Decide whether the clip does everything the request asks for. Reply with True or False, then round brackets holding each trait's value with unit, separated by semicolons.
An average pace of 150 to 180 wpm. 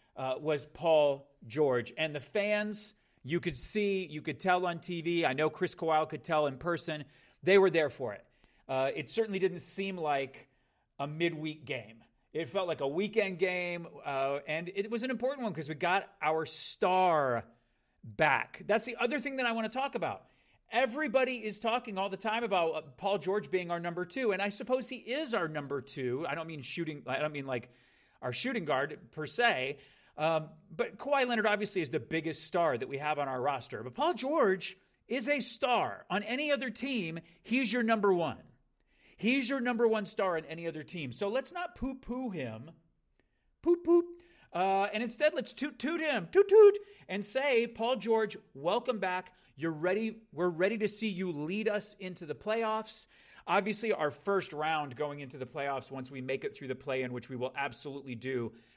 False (195 wpm)